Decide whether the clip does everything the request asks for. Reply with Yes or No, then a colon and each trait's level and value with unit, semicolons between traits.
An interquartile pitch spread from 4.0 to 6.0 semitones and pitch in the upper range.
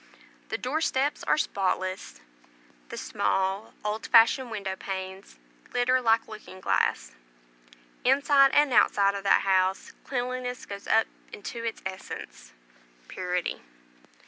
Yes: average, 4.9 semitones; high, 215 Hz